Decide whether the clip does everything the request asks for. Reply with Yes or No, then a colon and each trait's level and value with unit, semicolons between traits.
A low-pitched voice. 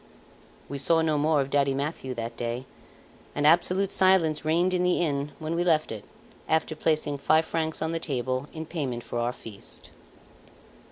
No: medium, 155 Hz